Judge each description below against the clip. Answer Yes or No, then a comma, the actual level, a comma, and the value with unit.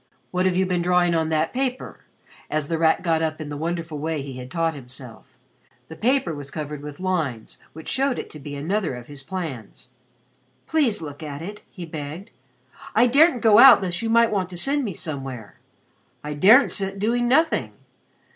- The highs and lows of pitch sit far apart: Yes, wide, 5.9 semitones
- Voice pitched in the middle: Yes, medium, 165 Hz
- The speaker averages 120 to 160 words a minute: No, average, 195 wpm